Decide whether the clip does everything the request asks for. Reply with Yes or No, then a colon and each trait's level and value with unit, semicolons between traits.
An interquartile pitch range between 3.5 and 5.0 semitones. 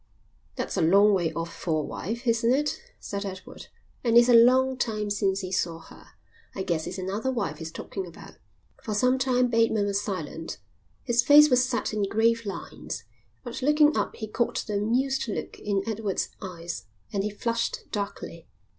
Yes: average, 4.1 semitones